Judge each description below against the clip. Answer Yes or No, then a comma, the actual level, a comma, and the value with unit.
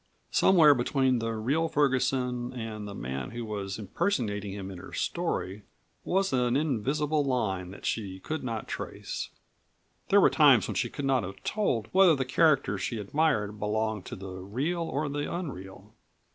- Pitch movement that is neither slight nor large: No, wide, 6.0 semitones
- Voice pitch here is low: Yes, low, 120 Hz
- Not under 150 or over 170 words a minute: Yes, average, 165 wpm